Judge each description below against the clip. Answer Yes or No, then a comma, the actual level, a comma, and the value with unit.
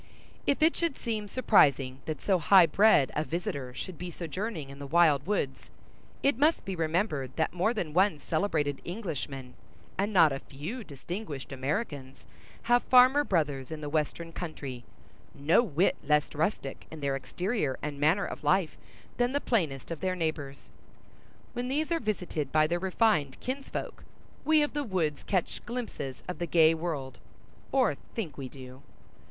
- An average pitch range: No, wide, 6.7 semitones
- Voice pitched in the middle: Yes, medium, 165 Hz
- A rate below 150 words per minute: No, average, 165 wpm